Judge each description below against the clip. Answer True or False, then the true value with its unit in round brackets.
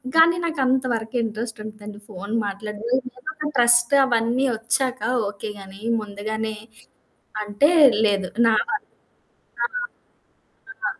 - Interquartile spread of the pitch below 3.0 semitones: False (3.6 semitones)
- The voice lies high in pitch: True (225 Hz)